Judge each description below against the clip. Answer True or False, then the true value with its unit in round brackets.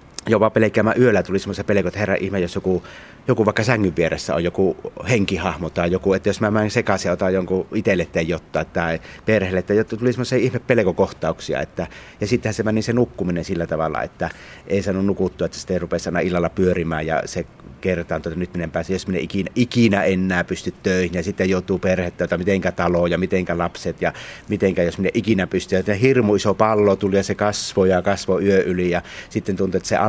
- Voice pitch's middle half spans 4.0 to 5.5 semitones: False (2.8 semitones)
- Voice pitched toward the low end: True (95 Hz)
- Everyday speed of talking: False (215 wpm)